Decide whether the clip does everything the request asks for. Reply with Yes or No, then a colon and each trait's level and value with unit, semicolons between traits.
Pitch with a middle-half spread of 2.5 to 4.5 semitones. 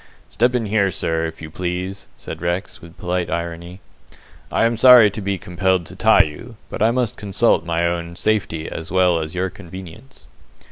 Yes: average, 3.7 semitones